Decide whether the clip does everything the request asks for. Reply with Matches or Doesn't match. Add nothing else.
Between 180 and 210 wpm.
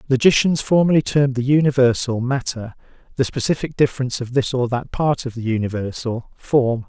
Doesn't match